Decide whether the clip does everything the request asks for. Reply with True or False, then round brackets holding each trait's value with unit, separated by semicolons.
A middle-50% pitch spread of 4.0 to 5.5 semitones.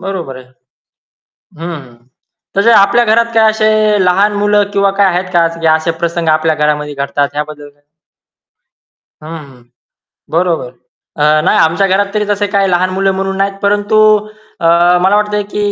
True (4.4 semitones)